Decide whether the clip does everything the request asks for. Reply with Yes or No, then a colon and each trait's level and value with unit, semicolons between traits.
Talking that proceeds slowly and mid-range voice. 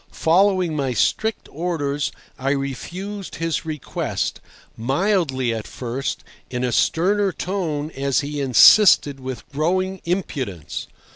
Yes: slow, 115 wpm; medium, 150 Hz